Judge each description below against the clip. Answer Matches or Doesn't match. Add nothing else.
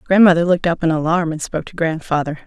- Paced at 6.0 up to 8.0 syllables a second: Matches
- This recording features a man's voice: Doesn't match